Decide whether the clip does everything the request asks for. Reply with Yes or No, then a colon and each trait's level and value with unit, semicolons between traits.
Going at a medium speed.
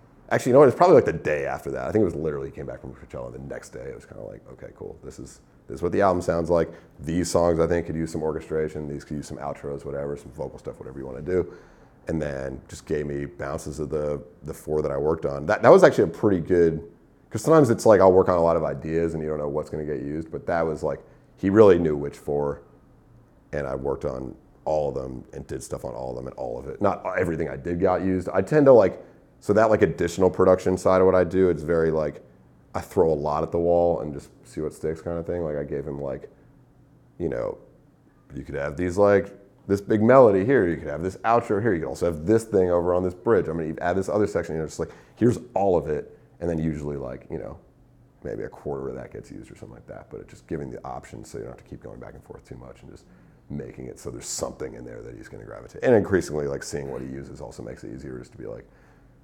No: fast, 285 wpm